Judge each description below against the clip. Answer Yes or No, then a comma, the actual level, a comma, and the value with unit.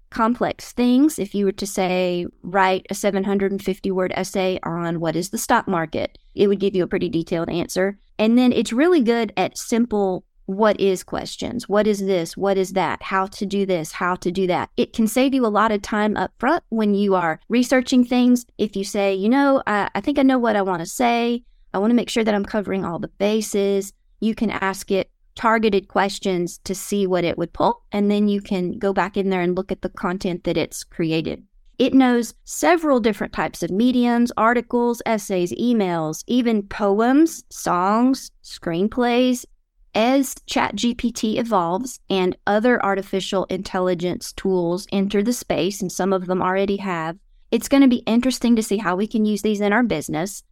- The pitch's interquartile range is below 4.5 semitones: Yes, average, 3.8 semitones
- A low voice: No, high, 200 Hz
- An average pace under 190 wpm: No, average, 195 wpm